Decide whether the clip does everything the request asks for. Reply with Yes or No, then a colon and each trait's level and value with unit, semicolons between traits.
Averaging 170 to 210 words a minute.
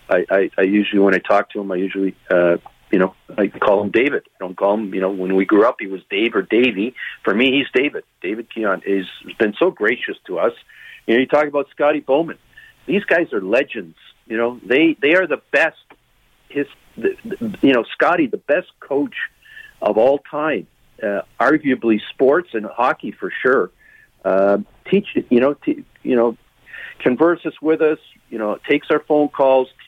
Yes: average, 200 wpm